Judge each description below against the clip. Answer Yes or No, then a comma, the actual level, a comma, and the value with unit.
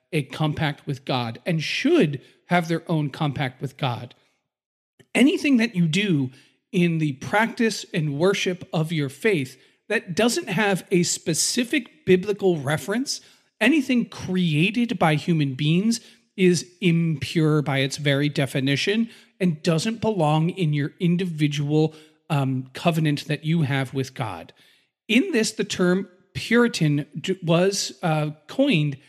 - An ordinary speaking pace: No, slow, 130 wpm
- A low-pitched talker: No, medium, 165 Hz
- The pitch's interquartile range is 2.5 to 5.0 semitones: No, wide, 5.4 semitones